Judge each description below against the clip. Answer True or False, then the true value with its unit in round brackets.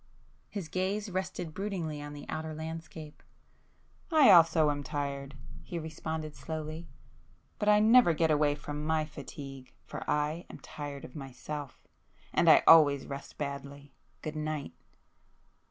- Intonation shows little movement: True (2.3 semitones)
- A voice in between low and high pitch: True (155 Hz)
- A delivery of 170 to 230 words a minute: False (135 wpm)